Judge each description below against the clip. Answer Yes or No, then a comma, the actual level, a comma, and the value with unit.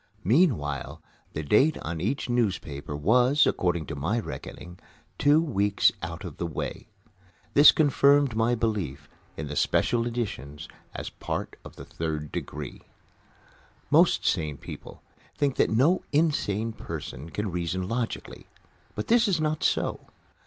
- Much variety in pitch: Yes, wide, 9.0 semitones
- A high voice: No, low, 105 Hz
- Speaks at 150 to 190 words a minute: No, average, 140 wpm